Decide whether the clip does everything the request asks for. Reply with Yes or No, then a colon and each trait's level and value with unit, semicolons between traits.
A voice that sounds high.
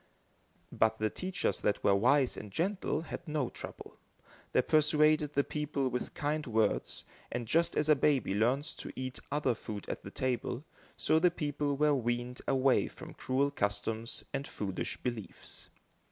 No: low, 135 Hz